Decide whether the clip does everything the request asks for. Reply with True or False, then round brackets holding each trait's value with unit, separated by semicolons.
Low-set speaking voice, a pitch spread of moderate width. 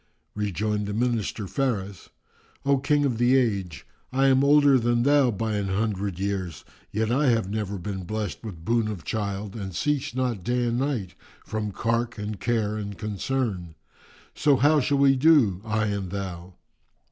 True (110 Hz; 4.2 semitones)